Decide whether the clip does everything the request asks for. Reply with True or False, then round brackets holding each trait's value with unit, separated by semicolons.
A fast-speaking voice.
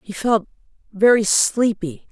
False (115 wpm)